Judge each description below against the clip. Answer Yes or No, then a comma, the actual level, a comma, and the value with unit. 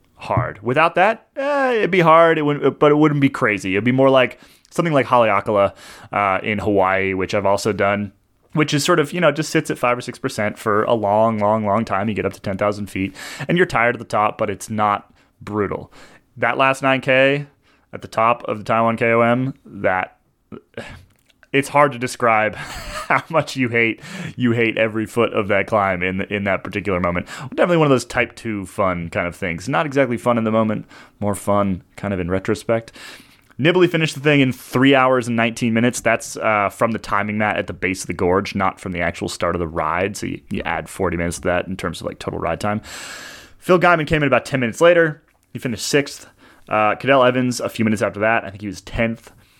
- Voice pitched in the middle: No, low, 115 Hz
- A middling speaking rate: No, fast, 225 wpm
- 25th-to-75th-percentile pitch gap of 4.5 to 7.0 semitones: Yes, average, 5.2 semitones